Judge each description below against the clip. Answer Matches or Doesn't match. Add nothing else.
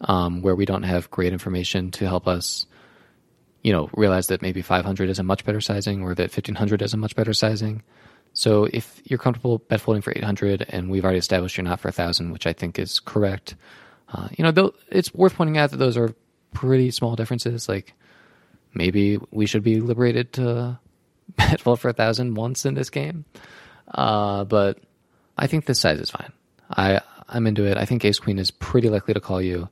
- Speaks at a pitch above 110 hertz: Doesn't match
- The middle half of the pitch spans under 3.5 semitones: Doesn't match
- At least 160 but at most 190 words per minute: Doesn't match